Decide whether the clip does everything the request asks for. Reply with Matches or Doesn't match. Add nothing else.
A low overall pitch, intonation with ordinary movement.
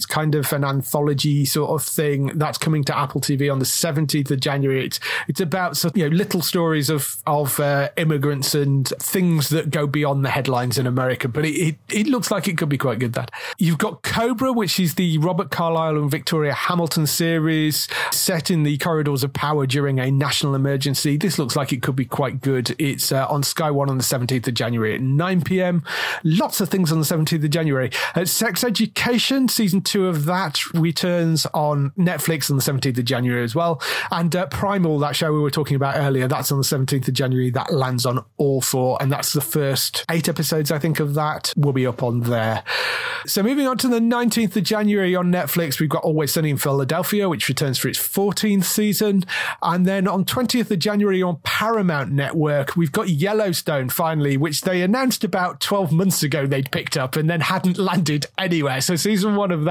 Doesn't match